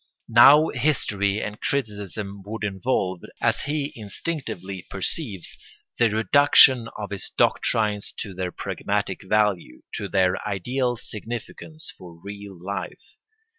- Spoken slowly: Yes, slow, 115 wpm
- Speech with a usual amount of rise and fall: Yes, average, 4.0 semitones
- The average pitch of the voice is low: Yes, low, 105 Hz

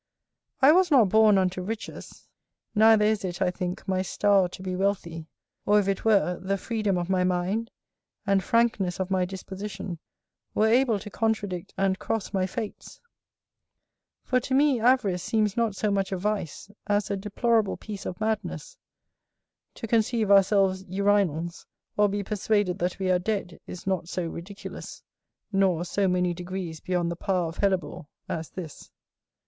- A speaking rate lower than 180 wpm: Yes, average, 165 wpm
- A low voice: No, high, 195 Hz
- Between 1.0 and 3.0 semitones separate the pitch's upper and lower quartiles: Yes, average, 2.7 semitones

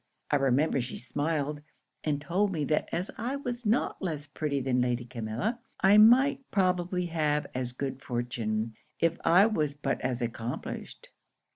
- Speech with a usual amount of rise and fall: No, wide, 6.6 semitones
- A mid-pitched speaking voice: Yes, medium, 150 Hz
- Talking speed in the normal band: Yes, average, 155 wpm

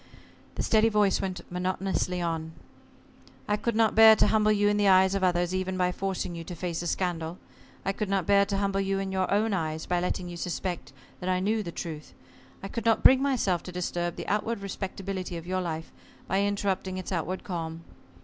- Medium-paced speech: No, fast, 210 wpm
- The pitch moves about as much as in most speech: No, narrow, 2.3 semitones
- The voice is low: No, medium, 185 Hz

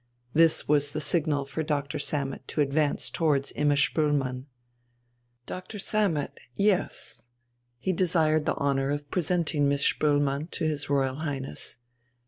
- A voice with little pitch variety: Yes, narrow, 2.2 semitones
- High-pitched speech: No, medium, 145 Hz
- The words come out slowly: Yes, slow, 130 wpm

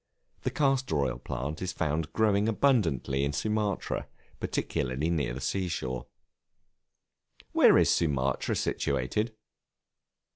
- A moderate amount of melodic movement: No, wide, 7.8 semitones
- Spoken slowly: Yes, slow, 110 wpm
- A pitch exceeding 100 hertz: No, very low, 80 Hz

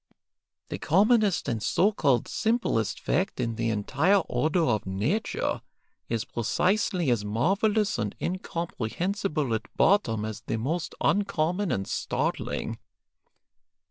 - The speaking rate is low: Yes, slow, 115 wpm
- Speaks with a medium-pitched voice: Yes, medium, 160 Hz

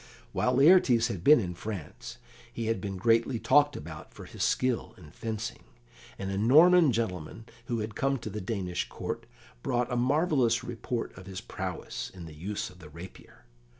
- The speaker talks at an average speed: Yes, average, 180 wpm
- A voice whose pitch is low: Yes, low, 115 Hz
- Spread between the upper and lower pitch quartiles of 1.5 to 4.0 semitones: No, average, 5.2 semitones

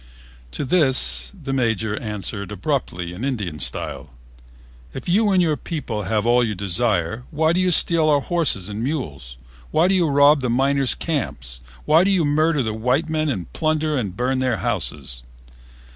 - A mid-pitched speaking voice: No, low, 130 Hz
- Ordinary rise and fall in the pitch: No, wide, 6.9 semitones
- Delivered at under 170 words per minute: No, average, 175 wpm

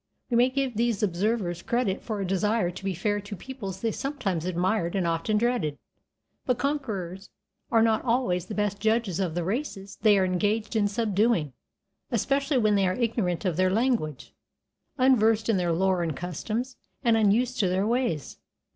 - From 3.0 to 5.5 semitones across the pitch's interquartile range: Yes, average, 4.3 semitones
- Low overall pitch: No, high, 210 Hz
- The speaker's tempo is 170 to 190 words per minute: Yes, average, 175 wpm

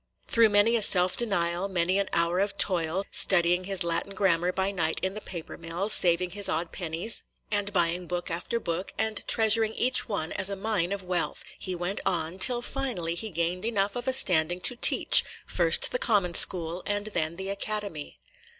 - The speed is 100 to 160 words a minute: No, average, 195 wpm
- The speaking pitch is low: No, high, 190 Hz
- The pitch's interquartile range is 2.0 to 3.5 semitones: Yes, average, 3.1 semitones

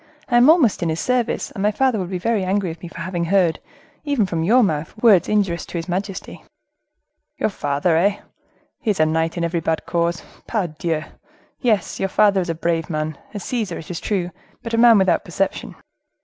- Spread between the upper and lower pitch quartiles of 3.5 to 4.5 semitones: Yes, average, 4.1 semitones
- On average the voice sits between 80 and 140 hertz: No, medium, 185 Hz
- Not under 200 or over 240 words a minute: Yes, fast, 205 wpm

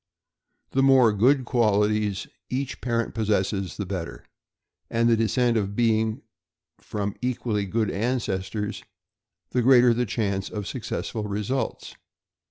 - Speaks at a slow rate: Yes, slow, 115 wpm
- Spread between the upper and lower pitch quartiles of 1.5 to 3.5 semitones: Yes, average, 3.1 semitones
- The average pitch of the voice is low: Yes, low, 110 Hz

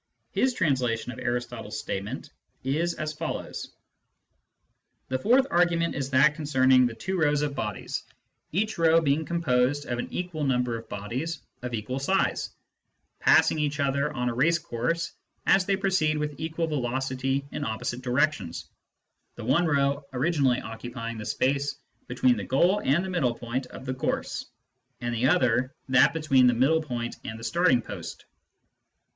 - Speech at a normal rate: Yes, average, 160 wpm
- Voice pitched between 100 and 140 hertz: Yes, low, 135 Hz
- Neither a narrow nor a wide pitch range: Yes, average, 4.5 semitones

